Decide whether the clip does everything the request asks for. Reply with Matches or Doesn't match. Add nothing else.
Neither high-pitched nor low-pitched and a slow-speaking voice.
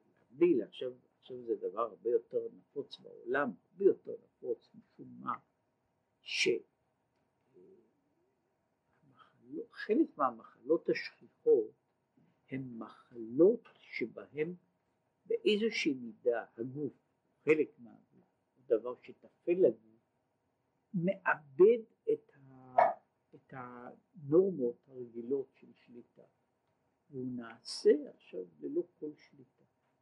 Doesn't match